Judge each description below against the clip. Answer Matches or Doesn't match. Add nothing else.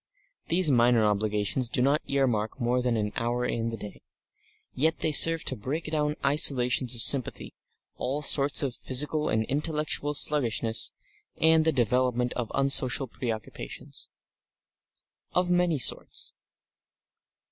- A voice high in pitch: Doesn't match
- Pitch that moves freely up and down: Doesn't match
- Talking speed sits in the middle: Doesn't match